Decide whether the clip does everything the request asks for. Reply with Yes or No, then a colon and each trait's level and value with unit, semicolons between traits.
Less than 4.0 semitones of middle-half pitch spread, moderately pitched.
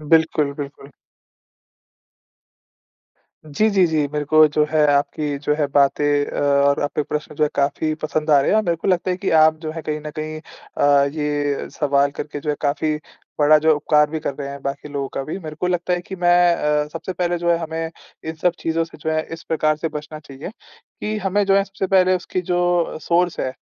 Yes: average, 2.7 semitones; medium, 155 Hz